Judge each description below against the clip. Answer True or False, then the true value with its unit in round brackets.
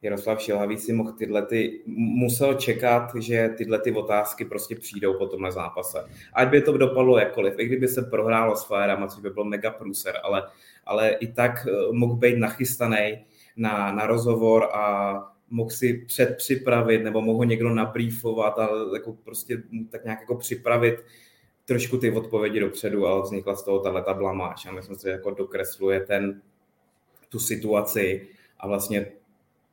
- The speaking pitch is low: True (110 Hz)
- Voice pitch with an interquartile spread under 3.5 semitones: True (2.7 semitones)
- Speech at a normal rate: True (160 wpm)